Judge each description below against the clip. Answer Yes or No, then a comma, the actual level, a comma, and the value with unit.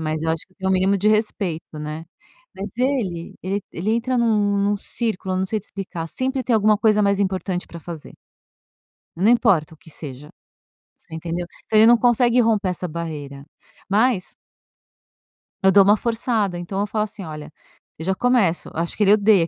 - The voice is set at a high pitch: Yes, high, 195 Hz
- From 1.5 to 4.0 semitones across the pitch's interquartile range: No, average, 4.4 semitones